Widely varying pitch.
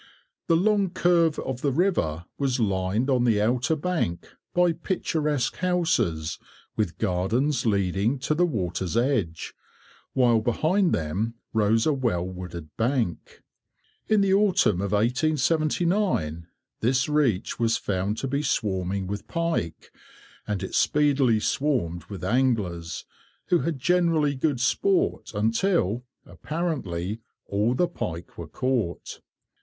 Yes: wide, 8.5 semitones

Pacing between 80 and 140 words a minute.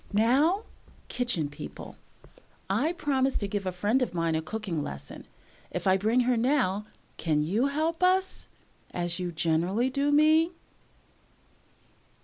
Yes: slow, 135 wpm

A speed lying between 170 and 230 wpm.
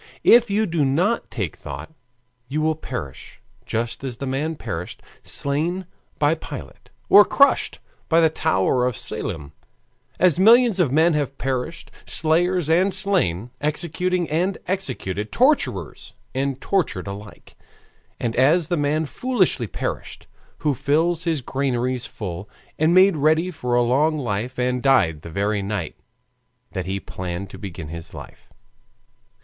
No: average, 145 wpm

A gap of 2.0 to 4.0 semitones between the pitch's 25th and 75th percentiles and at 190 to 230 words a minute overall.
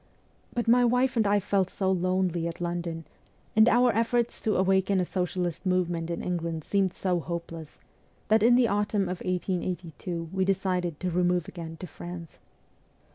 No: average, 2.7 semitones; average, 165 wpm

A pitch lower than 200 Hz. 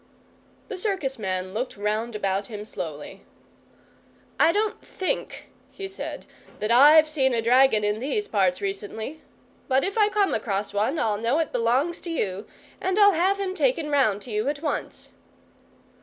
No: very high, 260 Hz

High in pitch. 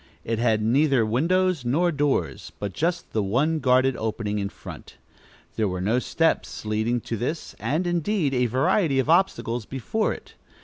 No: low, 130 Hz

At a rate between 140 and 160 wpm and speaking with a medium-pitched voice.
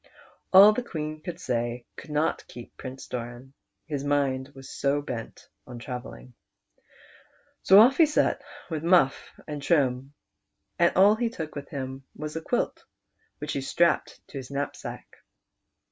Yes: average, 150 wpm; medium, 145 Hz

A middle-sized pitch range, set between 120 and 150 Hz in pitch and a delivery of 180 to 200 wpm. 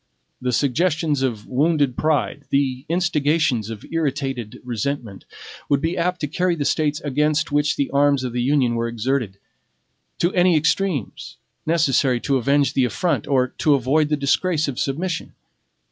No: average, 3.7 semitones; medium, 140 Hz; average, 155 wpm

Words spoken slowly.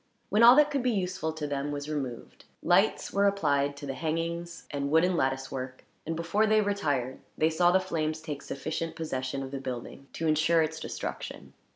No: average, 195 wpm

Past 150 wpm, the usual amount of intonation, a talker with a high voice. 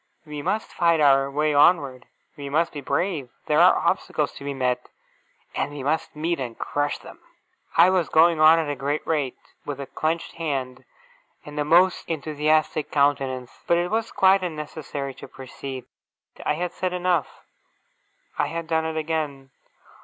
No: average, 170 wpm; average, 3.0 semitones; medium, 150 Hz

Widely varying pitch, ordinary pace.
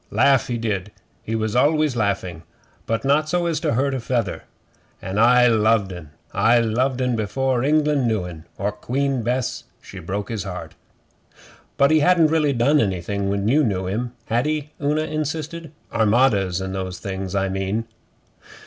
Yes: wide, 5.9 semitones; average, 170 wpm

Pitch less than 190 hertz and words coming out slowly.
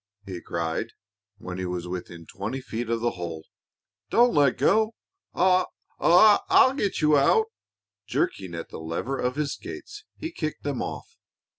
No: low, 135 Hz; average, 155 wpm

